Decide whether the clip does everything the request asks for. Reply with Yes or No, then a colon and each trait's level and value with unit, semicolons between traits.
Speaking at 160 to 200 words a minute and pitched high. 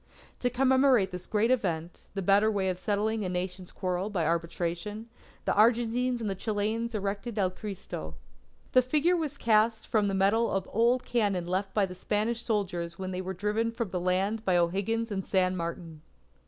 Yes: average, 180 wpm; high, 205 Hz